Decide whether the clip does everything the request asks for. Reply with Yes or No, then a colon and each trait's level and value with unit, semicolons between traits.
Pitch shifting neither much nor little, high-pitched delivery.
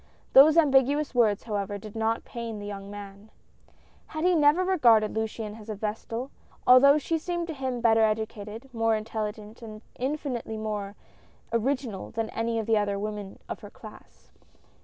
Yes: average, 3.9 semitones; high, 225 Hz